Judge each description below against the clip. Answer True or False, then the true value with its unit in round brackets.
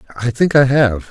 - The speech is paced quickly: True (215 wpm)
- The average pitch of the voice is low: True (130 Hz)